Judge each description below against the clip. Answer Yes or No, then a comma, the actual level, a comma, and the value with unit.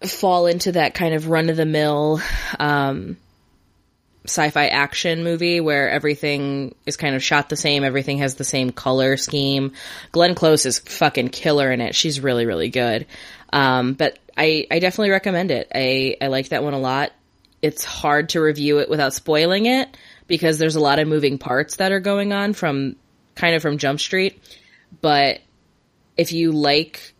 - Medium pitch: Yes, medium, 150 Hz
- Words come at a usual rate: Yes, average, 180 wpm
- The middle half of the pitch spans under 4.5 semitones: Yes, average, 3.3 semitones